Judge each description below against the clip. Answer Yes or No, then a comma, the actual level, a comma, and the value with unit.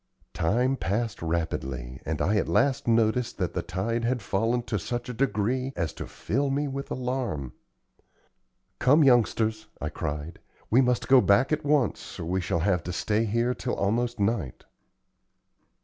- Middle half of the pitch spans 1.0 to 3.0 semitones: No, average, 5.0 semitones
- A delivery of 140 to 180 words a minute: Yes, average, 165 wpm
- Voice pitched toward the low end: Yes, low, 115 Hz